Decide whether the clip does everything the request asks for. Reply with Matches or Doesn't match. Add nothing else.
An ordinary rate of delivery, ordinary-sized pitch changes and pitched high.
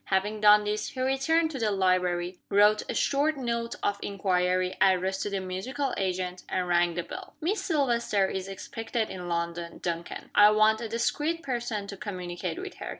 Matches